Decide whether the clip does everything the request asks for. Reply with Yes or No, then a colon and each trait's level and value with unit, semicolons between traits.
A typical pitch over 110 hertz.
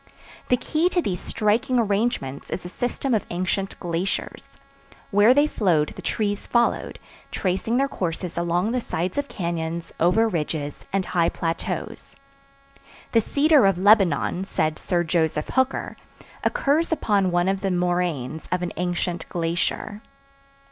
Yes: medium, 185 Hz